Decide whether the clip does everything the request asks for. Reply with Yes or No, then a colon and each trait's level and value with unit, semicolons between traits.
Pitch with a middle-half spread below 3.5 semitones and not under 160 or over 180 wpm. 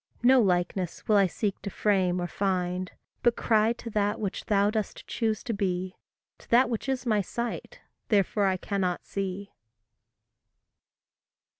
No: average, 3.1 semitones; average, 150 wpm